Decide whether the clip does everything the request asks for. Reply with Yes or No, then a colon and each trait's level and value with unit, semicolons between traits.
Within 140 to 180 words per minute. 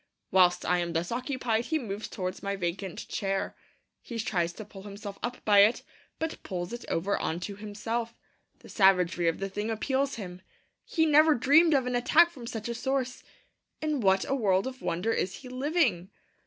No: average, 190 wpm